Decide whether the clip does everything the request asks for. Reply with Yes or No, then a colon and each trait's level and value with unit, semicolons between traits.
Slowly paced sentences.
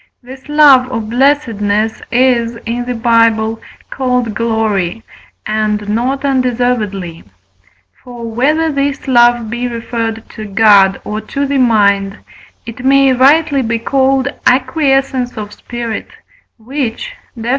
Yes: slow, 120 wpm